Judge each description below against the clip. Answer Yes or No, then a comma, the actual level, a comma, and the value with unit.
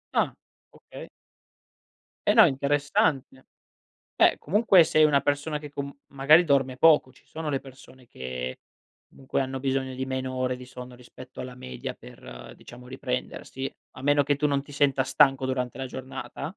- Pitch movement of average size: No, narrow, 2.0 semitones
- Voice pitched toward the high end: No, low, 135 Hz